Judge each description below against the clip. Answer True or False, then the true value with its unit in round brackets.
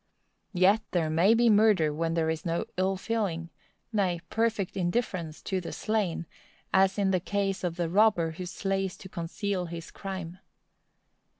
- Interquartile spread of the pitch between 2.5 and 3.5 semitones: True (3.2 semitones)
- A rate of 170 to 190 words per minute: False (145 wpm)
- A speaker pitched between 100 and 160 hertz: False (185 Hz)